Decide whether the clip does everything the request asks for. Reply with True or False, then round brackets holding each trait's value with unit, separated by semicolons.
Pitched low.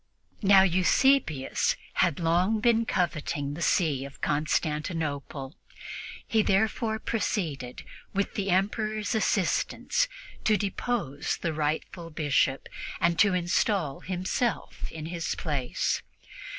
False (175 Hz)